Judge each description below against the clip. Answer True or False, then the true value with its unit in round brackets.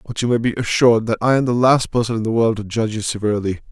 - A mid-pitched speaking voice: False (115 Hz)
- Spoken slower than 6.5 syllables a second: False (7.3 syllables/s)